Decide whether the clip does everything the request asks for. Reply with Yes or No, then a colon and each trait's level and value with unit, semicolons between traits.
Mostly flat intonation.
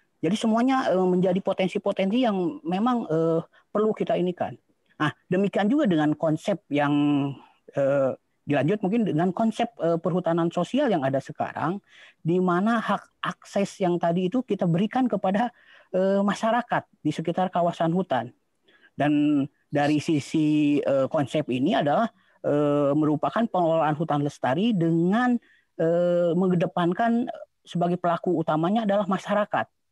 No: average, 4.6 semitones